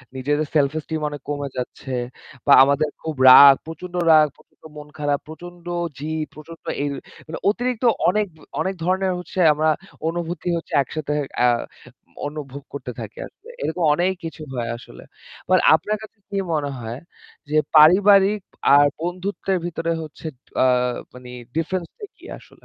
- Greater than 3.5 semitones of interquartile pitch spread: Yes, average, 4.0 semitones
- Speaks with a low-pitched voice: No, medium, 155 Hz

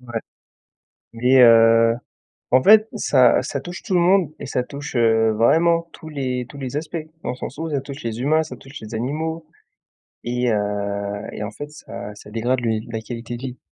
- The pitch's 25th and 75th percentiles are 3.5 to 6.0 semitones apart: Yes, average, 4.8 semitones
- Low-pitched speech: Yes, low, 125 Hz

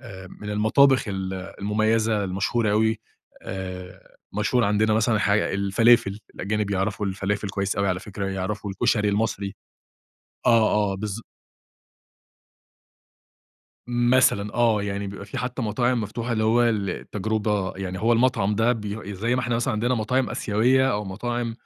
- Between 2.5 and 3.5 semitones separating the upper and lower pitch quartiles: Yes, average, 2.8 semitones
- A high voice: No, low, 105 Hz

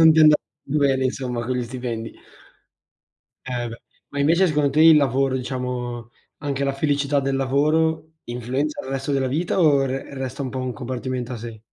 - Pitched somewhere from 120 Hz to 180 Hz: Yes, low, 135 Hz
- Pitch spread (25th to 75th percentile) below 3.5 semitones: Yes, narrow, 2.4 semitones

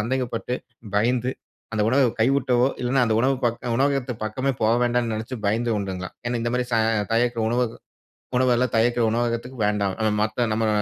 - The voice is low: Yes, low, 120 Hz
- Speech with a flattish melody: Yes, narrow, 2.0 semitones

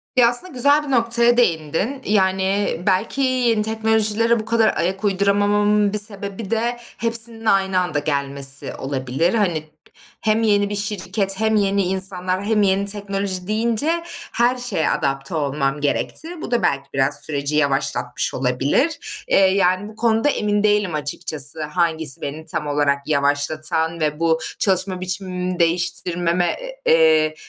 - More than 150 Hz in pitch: Yes, high, 190 Hz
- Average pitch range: No, wide, 5.7 semitones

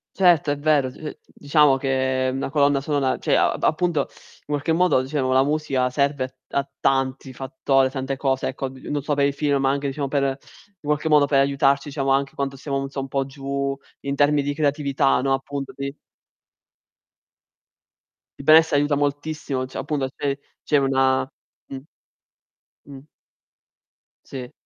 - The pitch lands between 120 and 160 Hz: Yes, medium, 140 Hz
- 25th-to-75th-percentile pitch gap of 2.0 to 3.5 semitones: No, narrow, 1.4 semitones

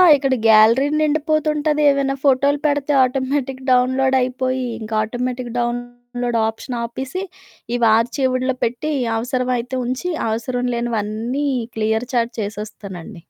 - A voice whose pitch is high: Yes, very high, 250 Hz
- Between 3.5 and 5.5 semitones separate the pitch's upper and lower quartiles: No, narrow, 2.5 semitones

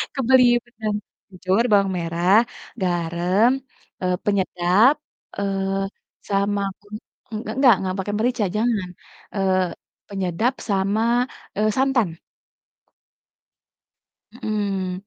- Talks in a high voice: Yes, high, 200 Hz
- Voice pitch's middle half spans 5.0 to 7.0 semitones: No, average, 3.0 semitones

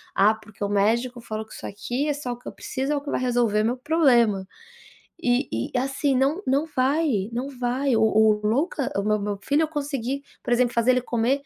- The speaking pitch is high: Yes, high, 245 Hz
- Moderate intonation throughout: Yes, average, 4.1 semitones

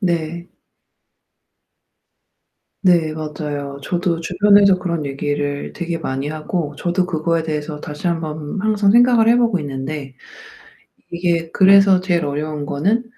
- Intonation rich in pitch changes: No, average, 3.9 semitones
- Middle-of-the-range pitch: Yes, medium, 165 Hz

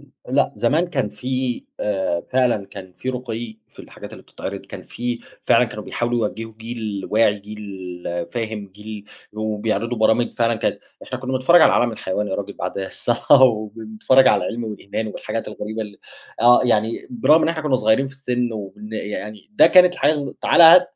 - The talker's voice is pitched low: Yes, low, 115 Hz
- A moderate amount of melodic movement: Yes, average, 3.4 semitones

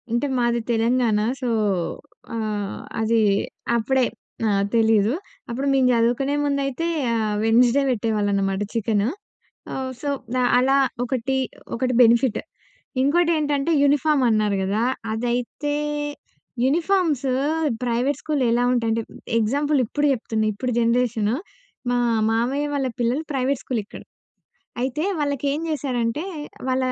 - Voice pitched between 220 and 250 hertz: Yes, high, 245 Hz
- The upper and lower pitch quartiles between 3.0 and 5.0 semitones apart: Yes, average, 3.6 semitones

